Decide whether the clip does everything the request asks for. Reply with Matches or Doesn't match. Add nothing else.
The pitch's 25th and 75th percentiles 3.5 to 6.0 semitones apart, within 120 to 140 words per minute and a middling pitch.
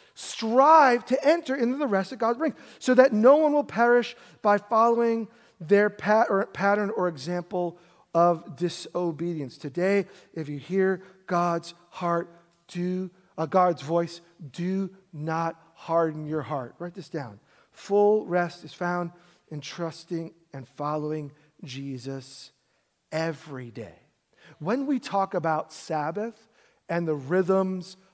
Matches